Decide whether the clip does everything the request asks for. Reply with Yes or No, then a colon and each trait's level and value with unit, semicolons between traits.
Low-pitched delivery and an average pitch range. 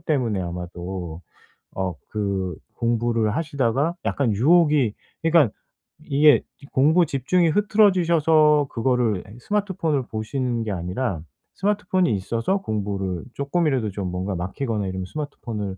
No: low, 120 Hz; wide, 7.6 semitones